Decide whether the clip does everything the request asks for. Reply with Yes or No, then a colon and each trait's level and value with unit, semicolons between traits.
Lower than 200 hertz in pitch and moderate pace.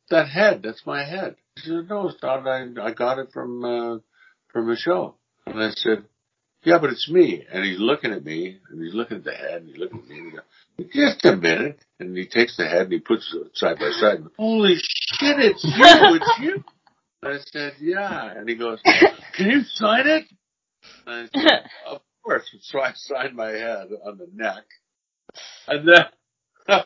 No: medium, 140 Hz; fast, 210 wpm